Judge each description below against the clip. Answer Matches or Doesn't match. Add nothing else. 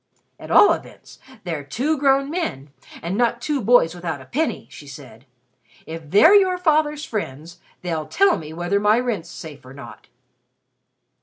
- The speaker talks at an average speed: Matches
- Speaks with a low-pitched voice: Doesn't match